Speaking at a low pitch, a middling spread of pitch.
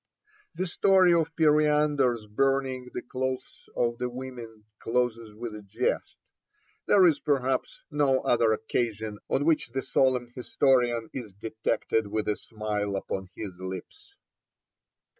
Yes: low, 125 Hz; average, 3.9 semitones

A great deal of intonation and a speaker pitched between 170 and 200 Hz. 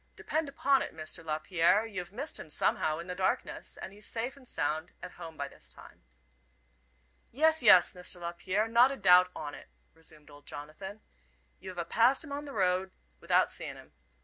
Yes: wide, 6.2 semitones; medium, 185 Hz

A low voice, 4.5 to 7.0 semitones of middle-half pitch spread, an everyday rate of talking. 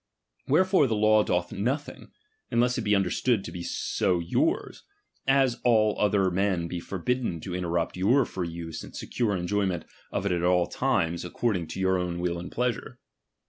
Yes: very low, 95 Hz; average, 5.3 semitones; average, 175 wpm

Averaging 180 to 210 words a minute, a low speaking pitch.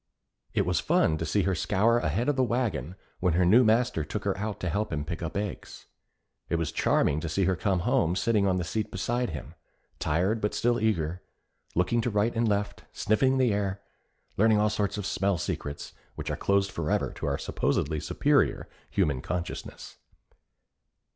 Yes: average, 185 wpm; low, 100 Hz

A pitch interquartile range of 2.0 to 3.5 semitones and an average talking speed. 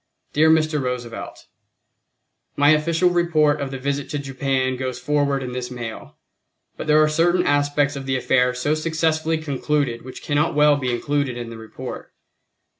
Yes: average, 3.1 semitones; average, 165 wpm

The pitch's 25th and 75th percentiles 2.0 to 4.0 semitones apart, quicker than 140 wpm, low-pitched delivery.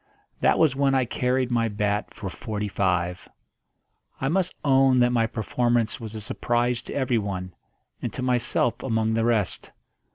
Yes: average, 3.1 semitones; average, 160 wpm; low, 120 Hz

